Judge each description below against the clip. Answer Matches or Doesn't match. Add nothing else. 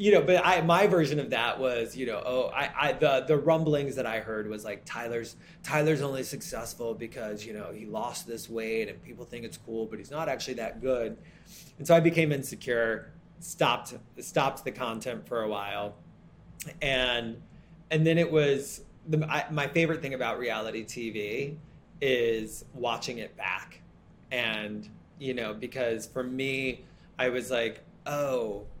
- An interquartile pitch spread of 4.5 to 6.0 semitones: Matches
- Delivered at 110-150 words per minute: Doesn't match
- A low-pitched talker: Matches